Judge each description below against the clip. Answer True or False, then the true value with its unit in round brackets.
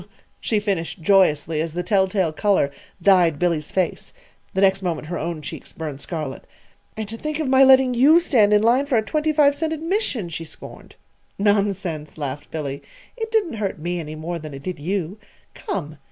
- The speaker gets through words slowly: False (190 wpm)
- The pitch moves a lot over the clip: True (6.9 semitones)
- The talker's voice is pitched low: False (190 Hz)